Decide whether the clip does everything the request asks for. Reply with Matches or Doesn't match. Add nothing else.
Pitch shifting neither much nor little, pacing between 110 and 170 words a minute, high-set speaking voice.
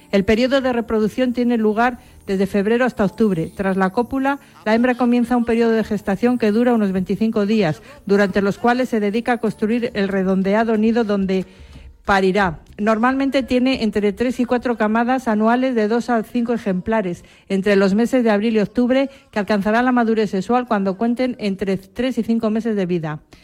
Doesn't match